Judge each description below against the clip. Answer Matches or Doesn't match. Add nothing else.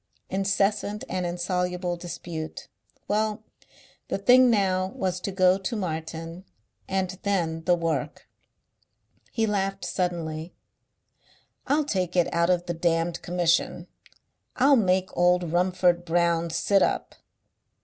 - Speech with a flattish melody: Matches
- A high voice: Doesn't match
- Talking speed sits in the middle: Doesn't match